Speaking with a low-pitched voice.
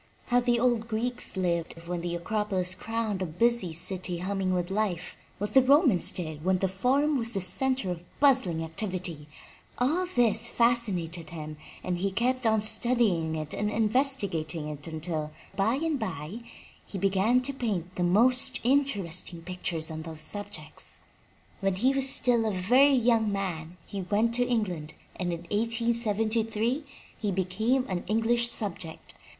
No: high, 205 Hz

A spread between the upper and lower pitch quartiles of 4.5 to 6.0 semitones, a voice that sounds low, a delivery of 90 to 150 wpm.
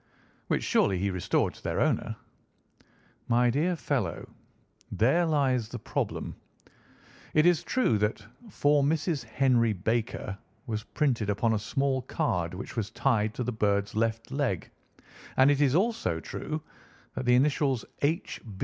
Yes: average, 5.0 semitones; low, 125 Hz; average, 145 wpm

